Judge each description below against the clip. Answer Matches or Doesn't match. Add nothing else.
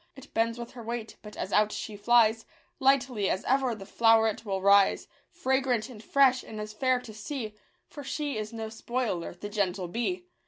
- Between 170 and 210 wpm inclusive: Matches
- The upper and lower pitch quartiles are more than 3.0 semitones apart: Matches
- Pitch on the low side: Doesn't match